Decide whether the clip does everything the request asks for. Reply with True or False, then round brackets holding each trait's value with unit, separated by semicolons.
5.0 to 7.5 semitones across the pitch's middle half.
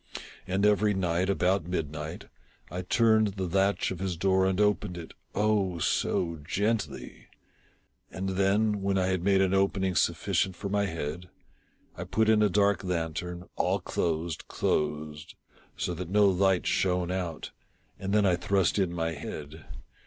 False (2.5 semitones)